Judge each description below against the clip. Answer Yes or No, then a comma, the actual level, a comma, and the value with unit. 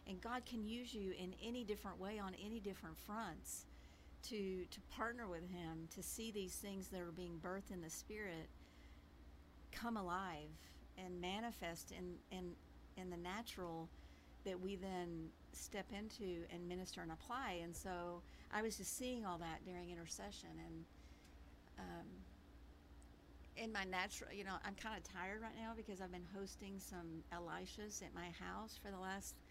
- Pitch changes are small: No, average, 3.7 semitones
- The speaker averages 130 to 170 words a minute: Yes, average, 165 wpm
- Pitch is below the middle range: No, medium, 180 Hz